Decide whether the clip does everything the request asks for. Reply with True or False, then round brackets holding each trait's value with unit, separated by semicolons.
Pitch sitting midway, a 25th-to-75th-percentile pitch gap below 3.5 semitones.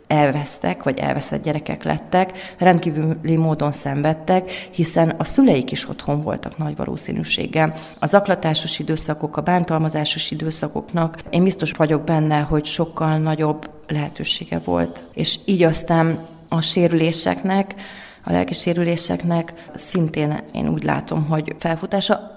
True (160 Hz; 2.4 semitones)